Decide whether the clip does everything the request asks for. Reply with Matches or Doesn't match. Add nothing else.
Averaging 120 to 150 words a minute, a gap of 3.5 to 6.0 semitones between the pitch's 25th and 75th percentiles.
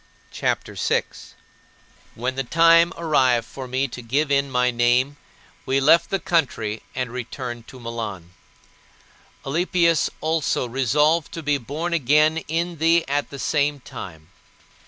Matches